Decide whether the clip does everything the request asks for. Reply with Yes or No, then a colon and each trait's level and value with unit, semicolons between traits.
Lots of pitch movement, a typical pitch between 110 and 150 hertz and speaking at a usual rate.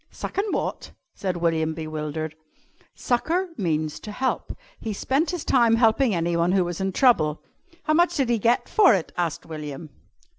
No: wide, 7.8 semitones; high, 190 Hz; average, 160 wpm